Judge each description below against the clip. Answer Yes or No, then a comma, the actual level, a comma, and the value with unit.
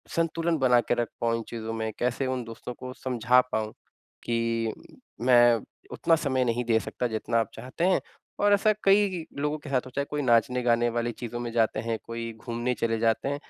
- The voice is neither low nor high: No, low, 120 Hz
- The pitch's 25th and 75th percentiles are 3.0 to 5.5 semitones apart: No, narrow, 2.4 semitones